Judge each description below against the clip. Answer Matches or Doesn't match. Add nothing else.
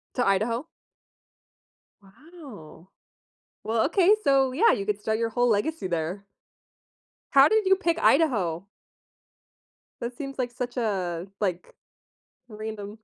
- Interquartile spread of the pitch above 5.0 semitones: Matches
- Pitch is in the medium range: Doesn't match